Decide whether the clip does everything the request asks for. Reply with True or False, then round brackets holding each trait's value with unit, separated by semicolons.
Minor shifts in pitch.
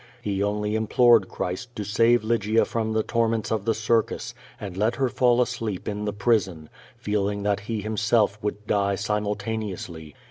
True (2.0 semitones)